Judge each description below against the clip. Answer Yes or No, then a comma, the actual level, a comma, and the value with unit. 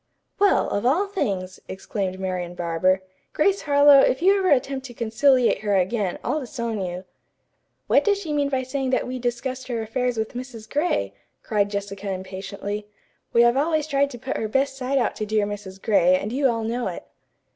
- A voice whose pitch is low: No, high, 235 Hz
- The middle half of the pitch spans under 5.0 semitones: No, wide, 5.5 semitones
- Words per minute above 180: Yes, average, 190 wpm